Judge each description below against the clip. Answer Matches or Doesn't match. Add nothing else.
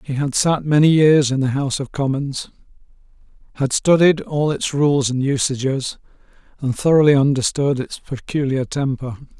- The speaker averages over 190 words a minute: Doesn't match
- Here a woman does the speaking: Doesn't match